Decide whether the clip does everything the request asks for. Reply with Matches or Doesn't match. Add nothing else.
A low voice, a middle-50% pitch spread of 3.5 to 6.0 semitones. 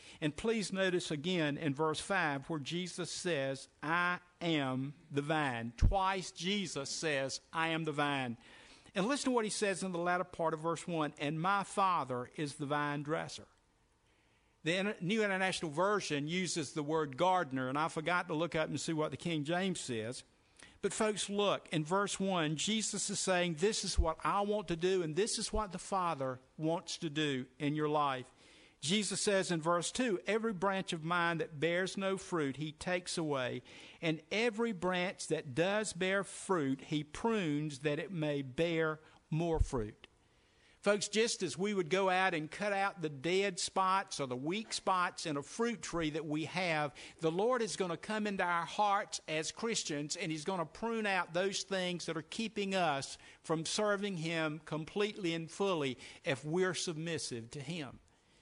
Doesn't match